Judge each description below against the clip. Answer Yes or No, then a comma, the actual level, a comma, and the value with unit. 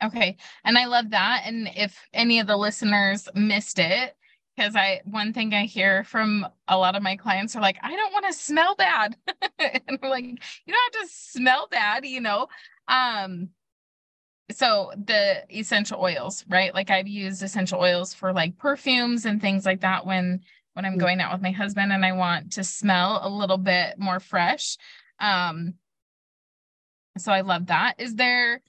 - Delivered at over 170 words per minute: Yes, average, 180 wpm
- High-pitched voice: Yes, high, 205 Hz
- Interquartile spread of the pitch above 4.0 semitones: Yes, average, 4.6 semitones